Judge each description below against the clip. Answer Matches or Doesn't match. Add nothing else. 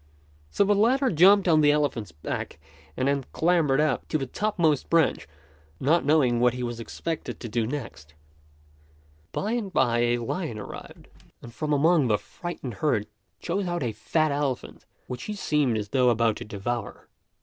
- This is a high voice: Doesn't match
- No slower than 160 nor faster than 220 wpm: Matches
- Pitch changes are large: Matches